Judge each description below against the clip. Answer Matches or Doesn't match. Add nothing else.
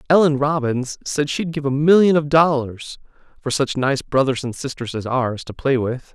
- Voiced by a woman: Doesn't match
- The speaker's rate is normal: Matches